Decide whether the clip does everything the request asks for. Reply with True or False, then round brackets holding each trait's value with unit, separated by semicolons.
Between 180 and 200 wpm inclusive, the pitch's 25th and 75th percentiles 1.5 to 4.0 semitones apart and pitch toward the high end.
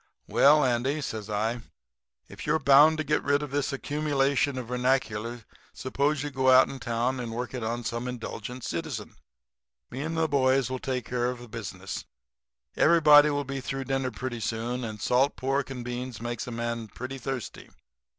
False (185 wpm; 2.8 semitones; 130 Hz)